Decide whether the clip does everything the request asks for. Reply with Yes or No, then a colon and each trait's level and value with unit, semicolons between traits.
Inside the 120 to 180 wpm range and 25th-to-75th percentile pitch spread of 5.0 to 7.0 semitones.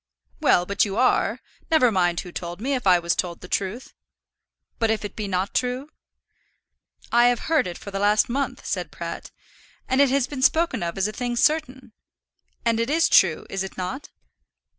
No: average, 195 wpm; wide, 5.4 semitones